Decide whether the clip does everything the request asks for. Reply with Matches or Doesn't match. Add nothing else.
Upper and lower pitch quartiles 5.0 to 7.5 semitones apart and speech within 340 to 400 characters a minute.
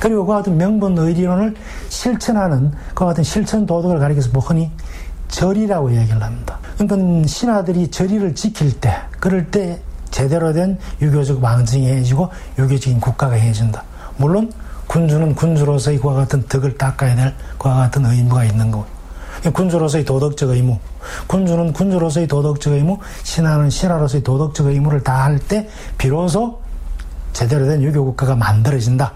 Matches